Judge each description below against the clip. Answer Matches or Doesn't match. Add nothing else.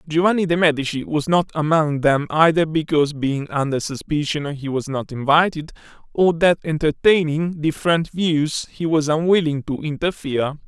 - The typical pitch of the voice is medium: Matches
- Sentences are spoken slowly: Doesn't match